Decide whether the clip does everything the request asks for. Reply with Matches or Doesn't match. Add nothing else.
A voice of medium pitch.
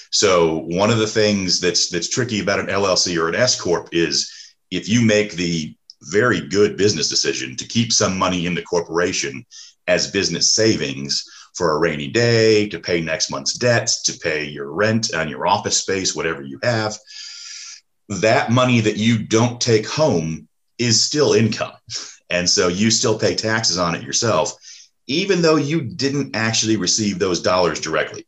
Doesn't match